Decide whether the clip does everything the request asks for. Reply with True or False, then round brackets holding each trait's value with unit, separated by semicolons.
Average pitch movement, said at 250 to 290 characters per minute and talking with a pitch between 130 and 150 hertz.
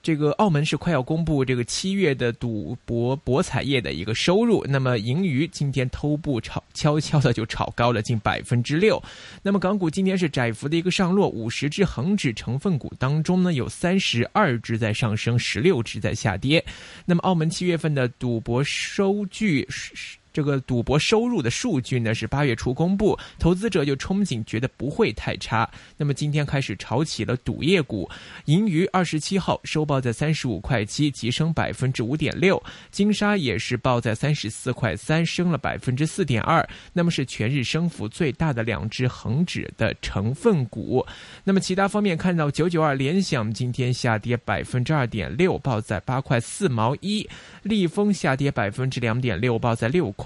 False (6.3 semitones; 285 characters per minute; 140 Hz)